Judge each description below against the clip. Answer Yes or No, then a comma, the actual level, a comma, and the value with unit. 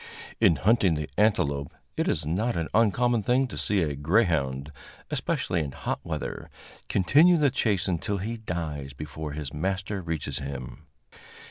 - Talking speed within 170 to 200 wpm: No, average, 150 wpm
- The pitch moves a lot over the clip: Yes, wide, 6.8 semitones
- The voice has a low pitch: Yes, very low, 85 Hz